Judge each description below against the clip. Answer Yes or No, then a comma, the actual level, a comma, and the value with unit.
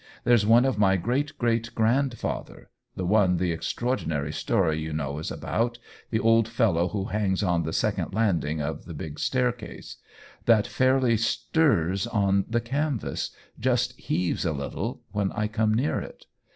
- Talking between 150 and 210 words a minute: Yes, average, 165 wpm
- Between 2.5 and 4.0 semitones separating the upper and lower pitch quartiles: No, average, 5.2 semitones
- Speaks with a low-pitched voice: Yes, low, 110 Hz